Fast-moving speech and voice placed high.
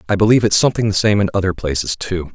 No: fast, 255 wpm; low, 100 Hz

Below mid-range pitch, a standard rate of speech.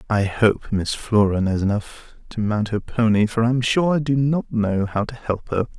No: low, 110 Hz; fast, 230 wpm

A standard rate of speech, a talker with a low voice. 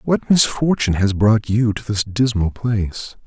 Yes: average, 165 wpm; low, 110 Hz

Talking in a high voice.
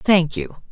No: medium, 175 Hz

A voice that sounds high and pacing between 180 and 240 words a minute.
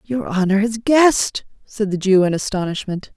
No: high, 205 Hz; average, 170 wpm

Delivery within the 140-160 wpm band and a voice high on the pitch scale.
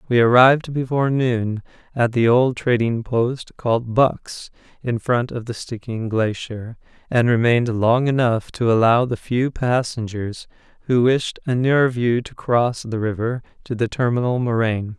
No: average, 155 wpm; low, 120 Hz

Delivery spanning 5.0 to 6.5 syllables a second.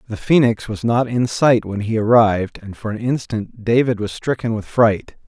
No: 4.8 syllables/s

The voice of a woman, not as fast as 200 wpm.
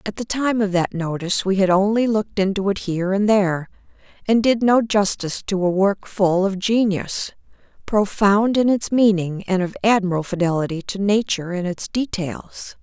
Yes: female; average, 180 wpm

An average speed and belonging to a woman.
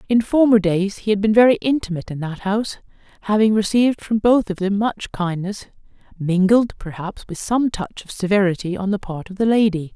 Yes: average, 195 wpm; female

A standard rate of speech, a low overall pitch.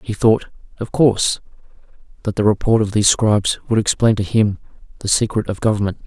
Yes: average, 180 wpm; low, 105 Hz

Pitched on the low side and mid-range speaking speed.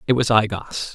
No: low, 115 Hz; fast, 255 wpm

